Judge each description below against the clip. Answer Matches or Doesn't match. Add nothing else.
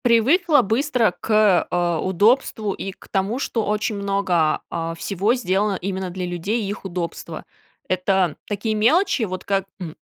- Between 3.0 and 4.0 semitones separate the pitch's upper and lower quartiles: Matches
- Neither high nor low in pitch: Doesn't match